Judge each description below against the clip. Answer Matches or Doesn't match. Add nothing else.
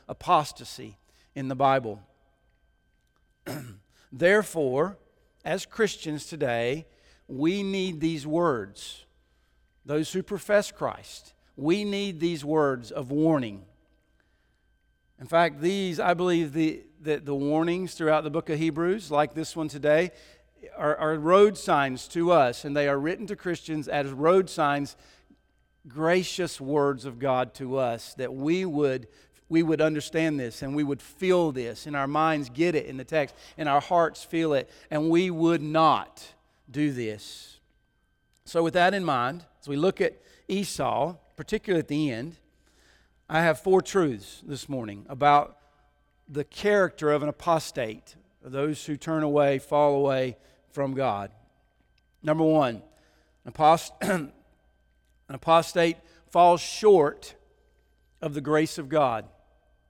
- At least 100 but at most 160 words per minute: Matches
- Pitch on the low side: Doesn't match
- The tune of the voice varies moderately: Matches